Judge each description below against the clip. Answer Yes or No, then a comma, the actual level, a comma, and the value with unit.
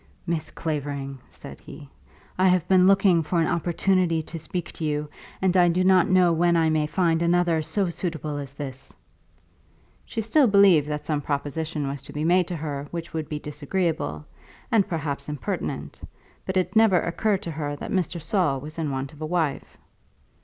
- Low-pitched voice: No, medium, 165 Hz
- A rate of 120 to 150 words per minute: No, average, 185 wpm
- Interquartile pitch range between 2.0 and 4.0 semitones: Yes, average, 3.5 semitones